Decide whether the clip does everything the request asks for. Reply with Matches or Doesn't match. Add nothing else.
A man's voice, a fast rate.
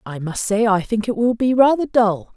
Doesn't match